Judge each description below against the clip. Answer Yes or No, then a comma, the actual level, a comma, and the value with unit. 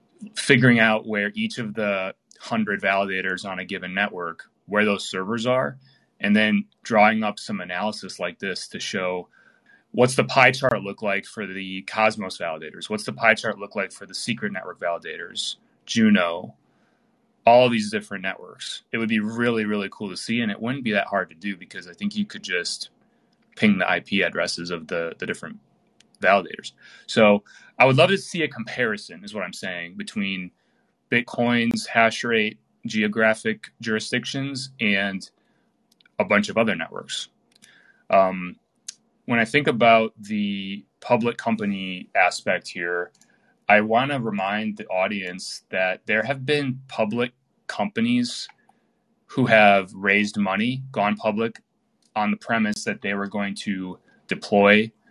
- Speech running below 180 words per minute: Yes, average, 160 wpm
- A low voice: Yes, low, 110 Hz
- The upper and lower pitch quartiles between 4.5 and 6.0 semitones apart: Yes, average, 4.8 semitones